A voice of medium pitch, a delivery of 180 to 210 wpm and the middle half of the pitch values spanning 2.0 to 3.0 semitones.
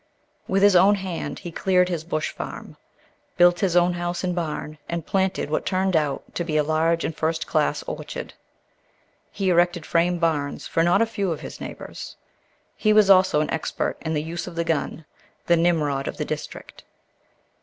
Yes: medium, 175 Hz; average, 185 wpm; narrow, 2.5 semitones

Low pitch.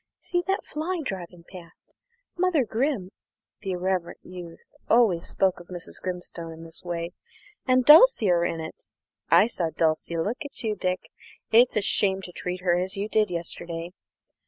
No: medium, 185 Hz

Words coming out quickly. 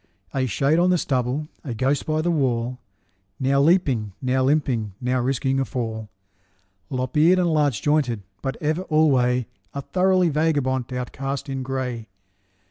No: average, 150 wpm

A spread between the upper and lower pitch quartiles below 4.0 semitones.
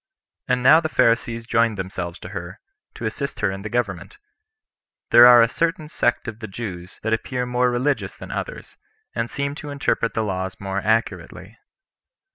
No: average, 4.4 semitones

